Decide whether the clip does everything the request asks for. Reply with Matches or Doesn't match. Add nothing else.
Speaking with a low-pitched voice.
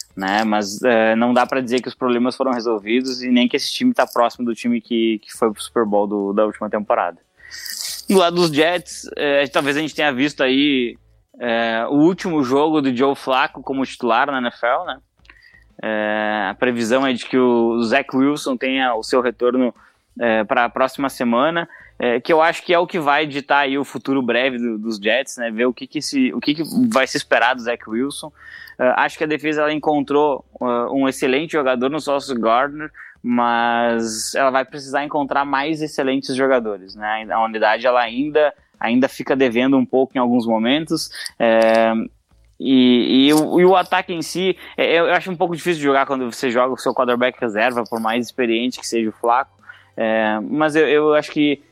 Matches